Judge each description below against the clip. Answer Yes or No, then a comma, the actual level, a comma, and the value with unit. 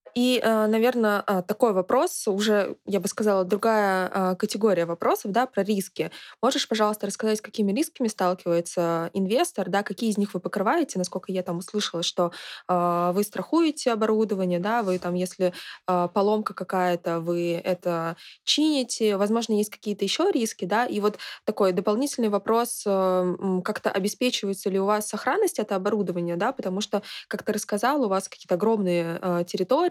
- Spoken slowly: No, average, 150 wpm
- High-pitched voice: Yes, high, 205 Hz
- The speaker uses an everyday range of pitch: Yes, average, 3.1 semitones